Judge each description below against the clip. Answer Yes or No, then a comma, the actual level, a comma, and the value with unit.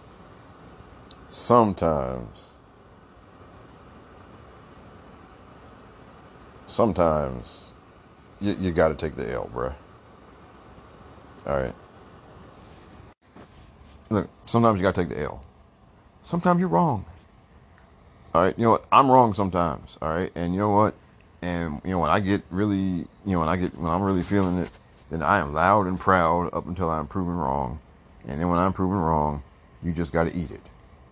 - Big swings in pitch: No, average, 3.7 semitones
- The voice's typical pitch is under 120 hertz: Yes, very low, 90 Hz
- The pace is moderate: Yes, average, 150 wpm